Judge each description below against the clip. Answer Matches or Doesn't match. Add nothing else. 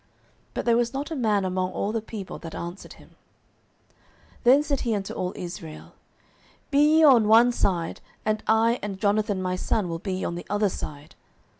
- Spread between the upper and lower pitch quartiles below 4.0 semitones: Doesn't match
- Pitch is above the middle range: Matches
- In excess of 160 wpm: Matches